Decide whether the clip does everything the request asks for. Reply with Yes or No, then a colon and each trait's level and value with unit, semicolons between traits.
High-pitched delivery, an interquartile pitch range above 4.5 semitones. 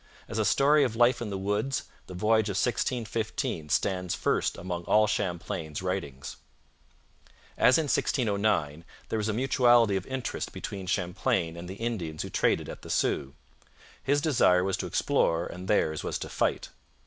No: low, 100 Hz; average, 4.9 semitones